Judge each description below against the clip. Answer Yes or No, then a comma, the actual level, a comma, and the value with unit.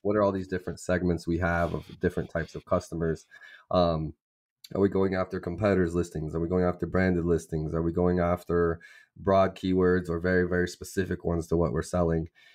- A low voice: Yes, very low, 90 Hz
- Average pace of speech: Yes, average, 195 wpm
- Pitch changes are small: Yes, narrow, 1.6 semitones